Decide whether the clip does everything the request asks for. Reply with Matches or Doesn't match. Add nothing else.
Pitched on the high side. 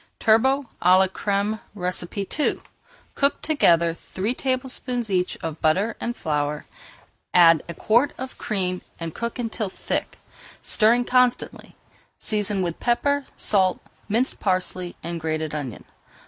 Matches